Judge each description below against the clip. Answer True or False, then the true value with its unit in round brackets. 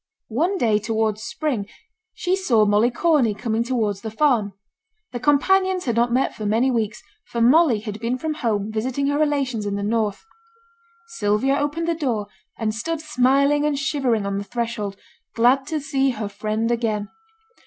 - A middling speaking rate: True (170 wpm)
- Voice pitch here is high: True (235 Hz)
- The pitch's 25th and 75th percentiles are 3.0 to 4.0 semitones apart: False (4.9 semitones)